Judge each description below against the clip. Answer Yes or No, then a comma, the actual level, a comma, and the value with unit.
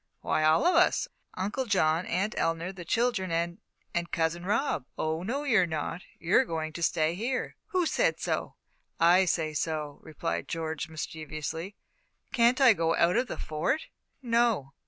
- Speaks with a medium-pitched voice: Yes, medium, 170 Hz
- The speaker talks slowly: No, average, 160 wpm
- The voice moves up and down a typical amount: No, wide, 6.4 semitones